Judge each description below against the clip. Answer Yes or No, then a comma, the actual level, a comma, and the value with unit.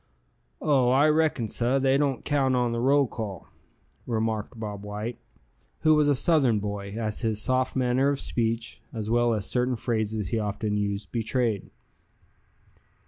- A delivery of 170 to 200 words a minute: No, average, 155 wpm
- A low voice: Yes, low, 115 Hz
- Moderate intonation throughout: Yes, average, 3.5 semitones